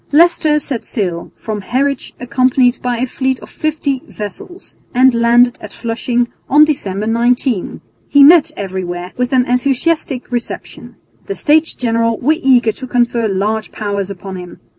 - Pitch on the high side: Yes, high, 245 Hz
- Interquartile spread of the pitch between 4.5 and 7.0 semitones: No, average, 4.0 semitones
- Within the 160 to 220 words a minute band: No, average, 150 wpm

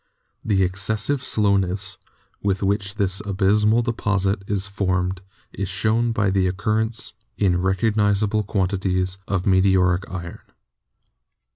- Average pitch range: No, narrow, 2.0 semitones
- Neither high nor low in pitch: No, low, 100 Hz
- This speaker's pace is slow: Yes, slow, 120 wpm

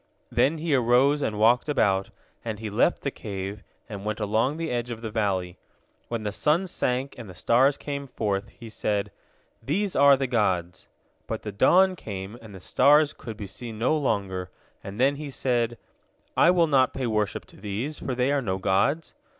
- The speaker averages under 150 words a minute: No, average, 190 wpm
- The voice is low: Yes, low, 120 Hz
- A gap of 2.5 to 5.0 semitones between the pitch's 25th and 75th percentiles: No, wide, 5.4 semitones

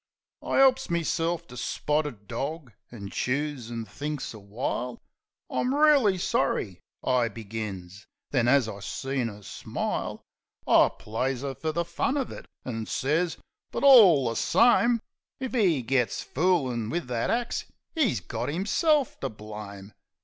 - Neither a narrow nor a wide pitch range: No, wide, 7.4 semitones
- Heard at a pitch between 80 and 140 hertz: Yes, low, 135 Hz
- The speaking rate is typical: Yes, average, 145 wpm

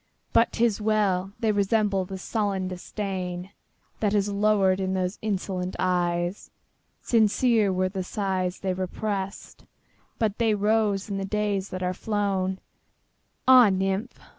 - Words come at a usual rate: No, slow, 115 wpm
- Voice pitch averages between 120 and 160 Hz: No, high, 195 Hz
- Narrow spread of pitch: Yes, narrow, 2.2 semitones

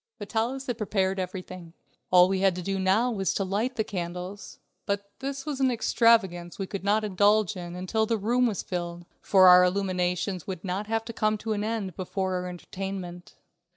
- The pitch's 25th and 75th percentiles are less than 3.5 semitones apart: Yes, average, 3.1 semitones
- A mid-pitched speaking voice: No, high, 195 Hz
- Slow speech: No, average, 195 wpm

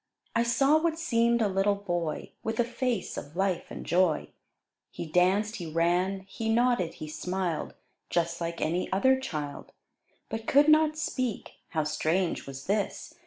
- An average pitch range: No, wide, 5.7 semitones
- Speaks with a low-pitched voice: No, high, 195 Hz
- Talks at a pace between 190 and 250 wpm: No, average, 160 wpm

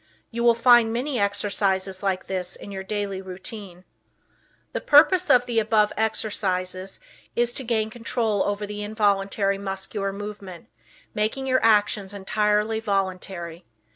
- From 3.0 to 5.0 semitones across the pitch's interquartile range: No, narrow, 2.6 semitones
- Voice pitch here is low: No, high, 205 Hz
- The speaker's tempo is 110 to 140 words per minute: Yes, slow, 135 wpm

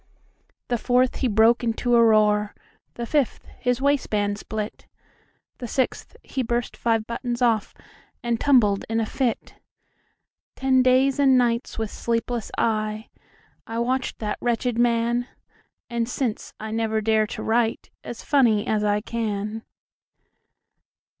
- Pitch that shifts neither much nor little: No, narrow, 2.1 semitones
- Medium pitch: No, high, 230 Hz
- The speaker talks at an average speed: No, slow, 115 wpm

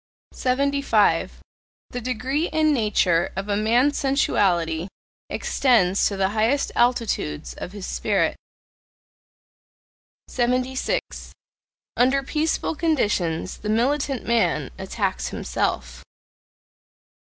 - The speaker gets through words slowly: Yes, slow, 90 wpm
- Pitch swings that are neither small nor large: No, wide, 5.7 semitones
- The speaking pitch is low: No, high, 240 Hz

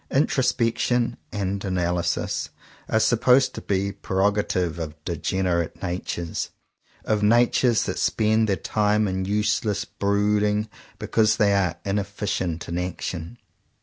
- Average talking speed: No, slow, 120 wpm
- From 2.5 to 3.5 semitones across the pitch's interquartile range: Yes, average, 3.0 semitones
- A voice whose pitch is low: Yes, low, 100 Hz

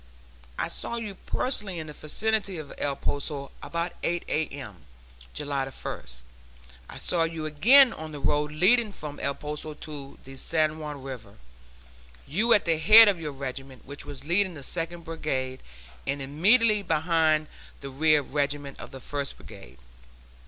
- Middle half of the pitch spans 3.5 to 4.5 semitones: Yes, average, 3.8 semitones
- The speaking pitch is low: No, medium, 155 Hz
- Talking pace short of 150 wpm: No, average, 160 wpm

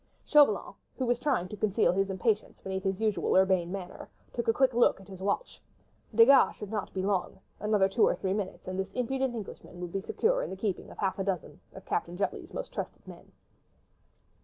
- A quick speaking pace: Yes, fast, 210 wpm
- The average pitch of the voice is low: No, high, 200 Hz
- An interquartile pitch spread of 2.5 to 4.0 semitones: Yes, average, 3.7 semitones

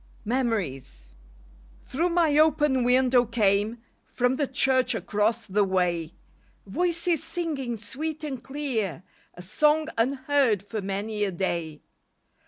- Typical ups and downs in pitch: No, wide, 6.2 semitones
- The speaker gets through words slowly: Yes, slow, 115 wpm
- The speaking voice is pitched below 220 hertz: No, high, 240 Hz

